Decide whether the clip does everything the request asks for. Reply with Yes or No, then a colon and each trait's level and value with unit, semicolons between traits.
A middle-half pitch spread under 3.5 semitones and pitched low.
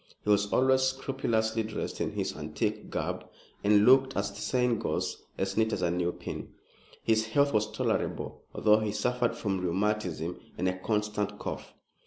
Yes: average, 2.8 semitones; low, 105 Hz